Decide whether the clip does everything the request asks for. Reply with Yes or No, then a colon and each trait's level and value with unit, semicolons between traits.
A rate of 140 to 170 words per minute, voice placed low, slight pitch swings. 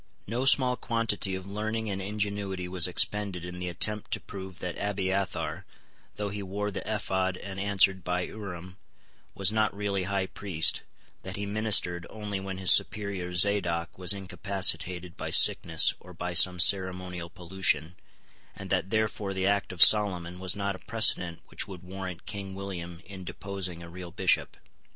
Yes: average, 165 wpm; very low, 95 Hz; narrow, 2.1 semitones